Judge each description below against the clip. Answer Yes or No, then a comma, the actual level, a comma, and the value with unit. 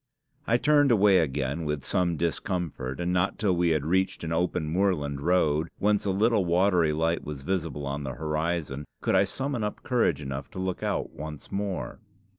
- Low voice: Yes, very low, 85 Hz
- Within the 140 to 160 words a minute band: No, average, 185 wpm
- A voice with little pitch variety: No, average, 4.2 semitones